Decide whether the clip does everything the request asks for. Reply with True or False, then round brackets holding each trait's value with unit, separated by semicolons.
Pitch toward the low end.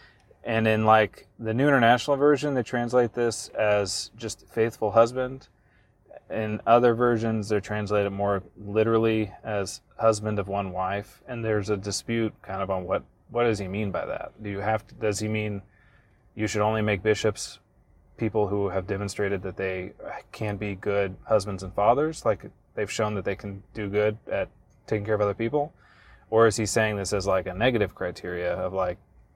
True (105 Hz)